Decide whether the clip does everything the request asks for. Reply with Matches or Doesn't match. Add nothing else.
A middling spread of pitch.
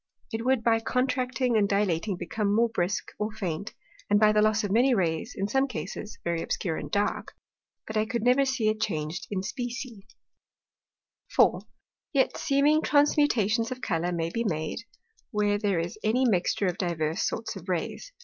Matches